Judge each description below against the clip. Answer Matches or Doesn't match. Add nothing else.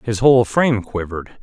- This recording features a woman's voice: Doesn't match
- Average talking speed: Matches